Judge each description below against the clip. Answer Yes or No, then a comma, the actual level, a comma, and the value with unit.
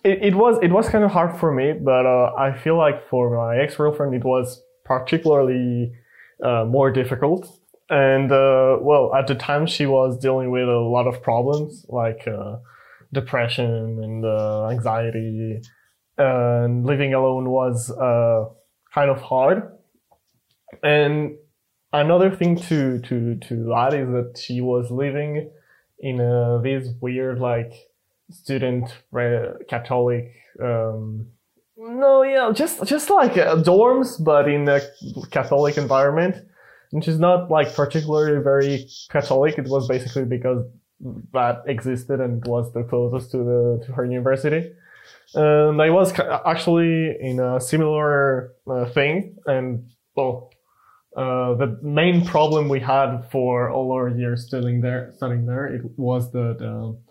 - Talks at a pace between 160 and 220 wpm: No, average, 145 wpm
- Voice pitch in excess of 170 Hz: No, low, 130 Hz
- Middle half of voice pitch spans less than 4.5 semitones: Yes, average, 3.4 semitones